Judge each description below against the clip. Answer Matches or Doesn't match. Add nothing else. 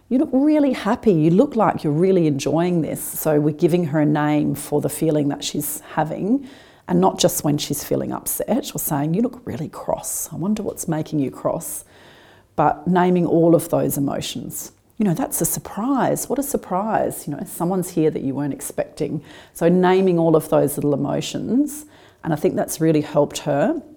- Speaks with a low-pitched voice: Doesn't match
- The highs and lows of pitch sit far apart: Matches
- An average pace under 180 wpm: Doesn't match